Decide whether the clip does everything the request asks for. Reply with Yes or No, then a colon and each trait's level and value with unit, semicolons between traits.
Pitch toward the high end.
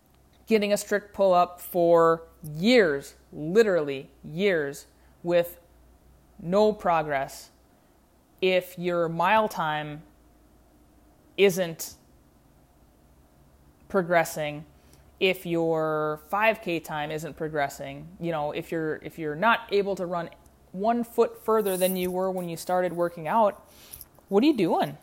No: medium, 170 Hz